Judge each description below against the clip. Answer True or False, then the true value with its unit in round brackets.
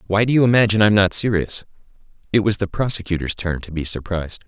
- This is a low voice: True (100 Hz)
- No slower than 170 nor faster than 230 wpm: True (200 wpm)